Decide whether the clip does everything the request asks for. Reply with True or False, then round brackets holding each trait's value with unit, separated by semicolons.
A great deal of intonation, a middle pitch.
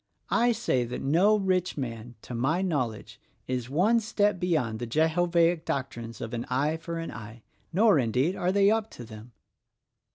True (7.2 semitones; 155 Hz)